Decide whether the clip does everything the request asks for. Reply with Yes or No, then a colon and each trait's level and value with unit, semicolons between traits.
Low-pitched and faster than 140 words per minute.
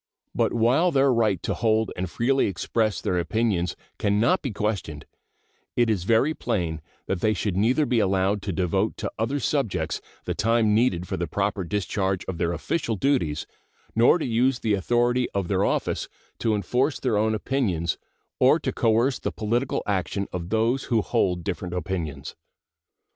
Yes: low, 105 Hz; average, 170 wpm